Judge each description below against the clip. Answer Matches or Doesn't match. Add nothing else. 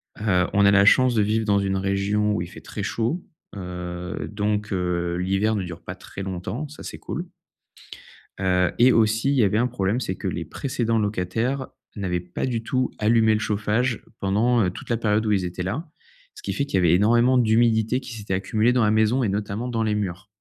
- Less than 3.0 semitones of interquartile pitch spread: Doesn't match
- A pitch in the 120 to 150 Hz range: Doesn't match